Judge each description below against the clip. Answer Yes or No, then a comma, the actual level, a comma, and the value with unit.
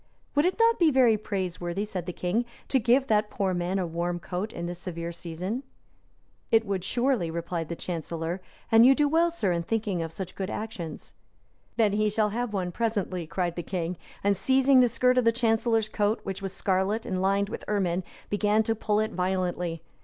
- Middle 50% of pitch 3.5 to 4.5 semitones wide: Yes, average, 4.2 semitones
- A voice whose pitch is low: No, high, 200 Hz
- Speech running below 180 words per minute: No, average, 200 wpm